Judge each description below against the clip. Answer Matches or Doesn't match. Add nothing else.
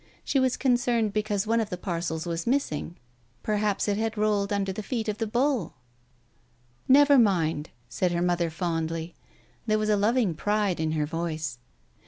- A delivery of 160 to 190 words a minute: Matches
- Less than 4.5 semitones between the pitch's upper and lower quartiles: Doesn't match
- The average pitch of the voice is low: Doesn't match